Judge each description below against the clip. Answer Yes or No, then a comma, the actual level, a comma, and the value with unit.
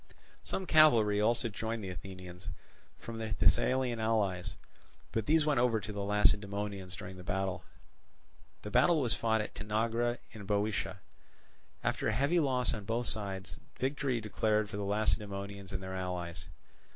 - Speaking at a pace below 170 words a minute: Yes, average, 150 wpm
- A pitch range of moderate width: Yes, average, 3.0 semitones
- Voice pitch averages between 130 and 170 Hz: No, low, 105 Hz